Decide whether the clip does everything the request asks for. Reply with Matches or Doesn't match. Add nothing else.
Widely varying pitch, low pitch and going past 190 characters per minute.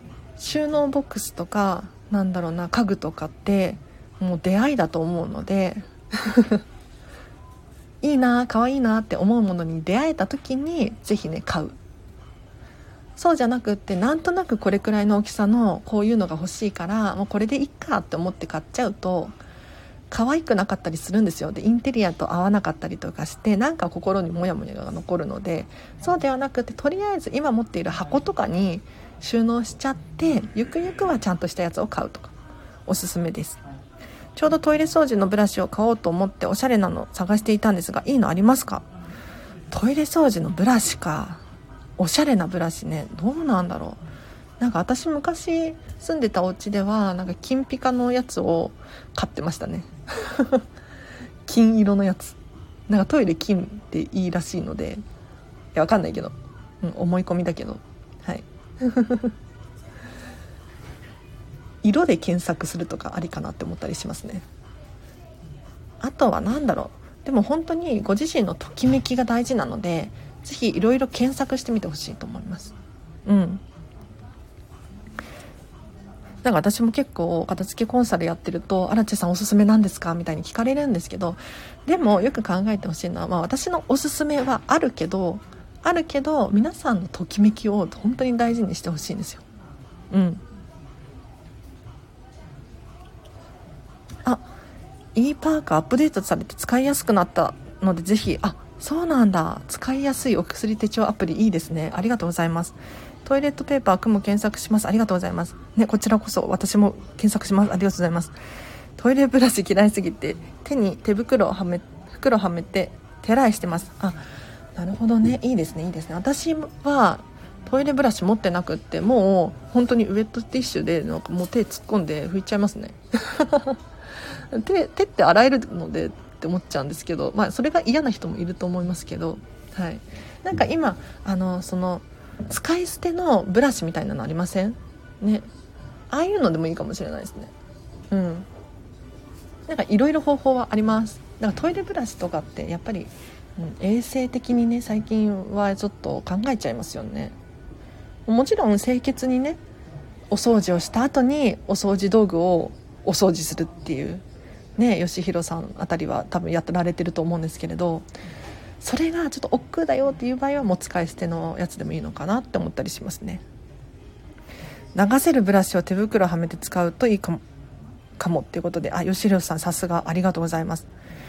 Doesn't match